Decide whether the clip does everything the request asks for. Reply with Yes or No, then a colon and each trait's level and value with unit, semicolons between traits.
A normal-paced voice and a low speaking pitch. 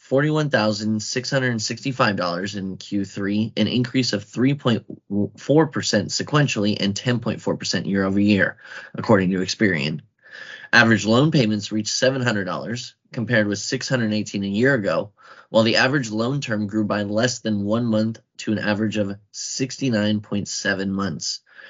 No: slow, 120 wpm; low, 110 Hz